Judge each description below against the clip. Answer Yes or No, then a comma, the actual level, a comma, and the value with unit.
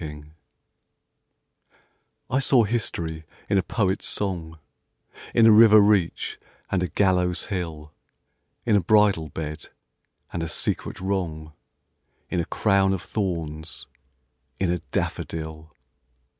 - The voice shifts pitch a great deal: No, average, 4.1 semitones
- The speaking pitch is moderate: No, very low, 90 Hz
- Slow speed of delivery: Yes, slow, 115 wpm